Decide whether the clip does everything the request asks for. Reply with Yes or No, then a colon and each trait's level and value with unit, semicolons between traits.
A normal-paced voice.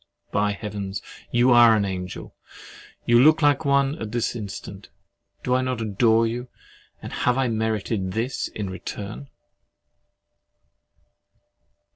No: slow, 115 wpm